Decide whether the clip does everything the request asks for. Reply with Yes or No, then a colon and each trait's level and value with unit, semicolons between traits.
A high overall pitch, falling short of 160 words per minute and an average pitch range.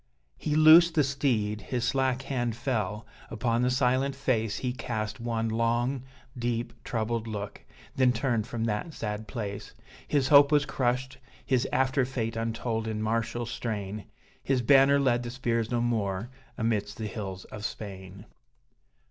No: low, 120 Hz; average, 150 wpm; average, 3.0 semitones